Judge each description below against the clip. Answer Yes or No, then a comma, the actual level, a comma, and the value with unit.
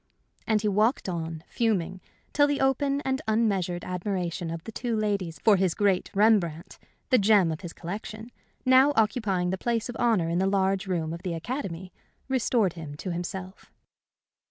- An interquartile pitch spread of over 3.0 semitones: Yes, average, 4.3 semitones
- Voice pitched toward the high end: Yes, high, 195 Hz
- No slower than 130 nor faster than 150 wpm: No, average, 170 wpm